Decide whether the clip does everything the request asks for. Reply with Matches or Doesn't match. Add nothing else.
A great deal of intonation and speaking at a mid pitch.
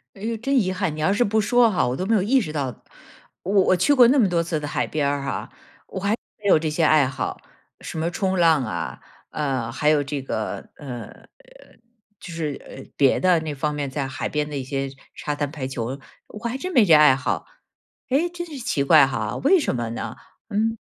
Matches